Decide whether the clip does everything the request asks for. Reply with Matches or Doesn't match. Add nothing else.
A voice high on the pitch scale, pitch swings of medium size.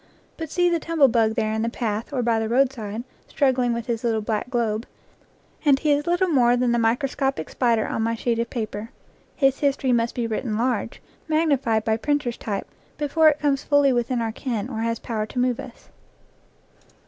Matches